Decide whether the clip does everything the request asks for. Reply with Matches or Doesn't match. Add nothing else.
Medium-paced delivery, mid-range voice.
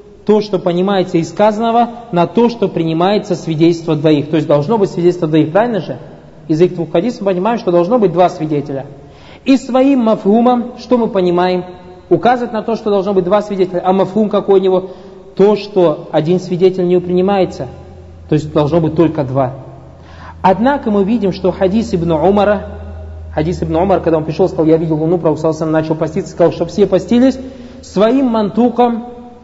Doesn't match